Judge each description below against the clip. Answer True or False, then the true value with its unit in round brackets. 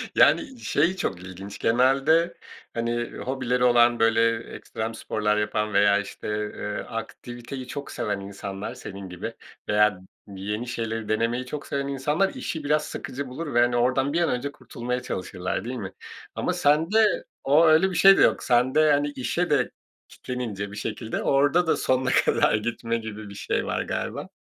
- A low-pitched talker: True (120 Hz)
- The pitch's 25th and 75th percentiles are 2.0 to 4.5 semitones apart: False (5.0 semitones)